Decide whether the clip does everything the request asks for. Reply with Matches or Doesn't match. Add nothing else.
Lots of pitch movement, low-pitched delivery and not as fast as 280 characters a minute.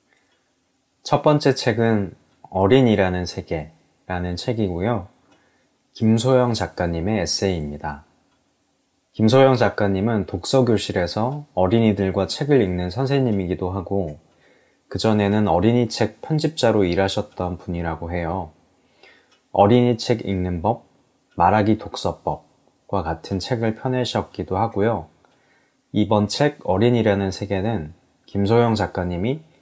Doesn't match